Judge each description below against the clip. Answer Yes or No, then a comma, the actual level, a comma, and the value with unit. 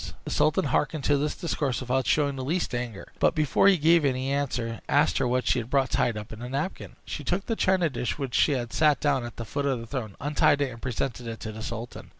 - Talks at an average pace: No, fast, 260 wpm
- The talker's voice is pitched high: No, low, 135 Hz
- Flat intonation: No, average, 3.6 semitones